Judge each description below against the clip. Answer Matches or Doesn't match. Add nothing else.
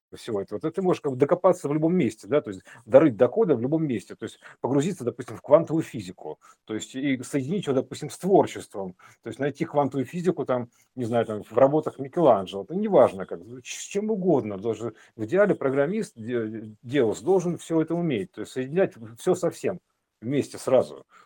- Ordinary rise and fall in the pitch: Doesn't match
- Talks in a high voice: Doesn't match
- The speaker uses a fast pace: Matches